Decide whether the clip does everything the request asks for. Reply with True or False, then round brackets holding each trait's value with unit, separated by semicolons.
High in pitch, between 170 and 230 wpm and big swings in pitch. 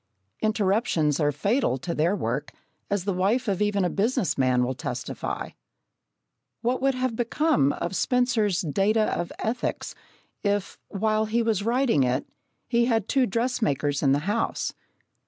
False (205 Hz; 150 wpm; 6.3 semitones)